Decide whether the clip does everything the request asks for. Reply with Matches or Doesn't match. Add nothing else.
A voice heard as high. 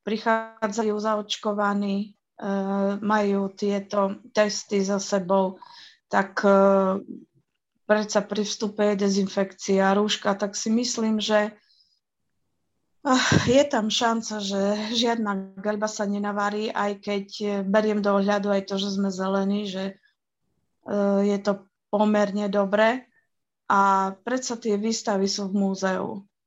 Matches